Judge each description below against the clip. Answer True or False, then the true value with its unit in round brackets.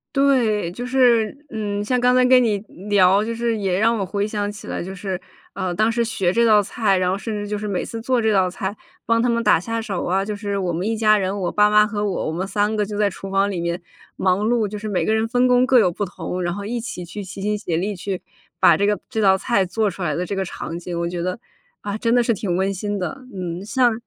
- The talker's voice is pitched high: True (205 Hz)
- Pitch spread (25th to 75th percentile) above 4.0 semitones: False (3.1 semitones)